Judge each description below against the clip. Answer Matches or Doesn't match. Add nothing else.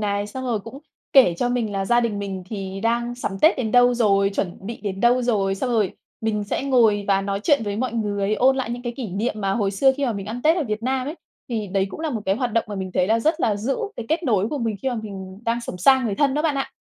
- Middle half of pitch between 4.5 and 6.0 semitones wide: Doesn't match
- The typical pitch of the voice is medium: Doesn't match